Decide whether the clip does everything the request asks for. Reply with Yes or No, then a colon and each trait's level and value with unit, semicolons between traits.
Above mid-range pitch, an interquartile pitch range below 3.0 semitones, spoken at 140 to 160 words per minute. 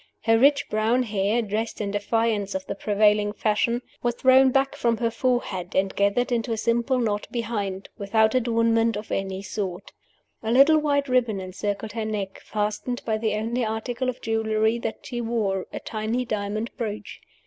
No: high, 220 Hz; narrow, 2.5 semitones; average, 170 wpm